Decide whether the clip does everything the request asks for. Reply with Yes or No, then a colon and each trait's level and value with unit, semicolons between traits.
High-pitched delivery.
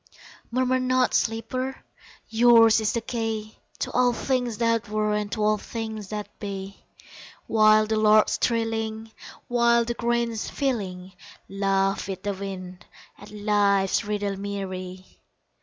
Yes: high, 215 Hz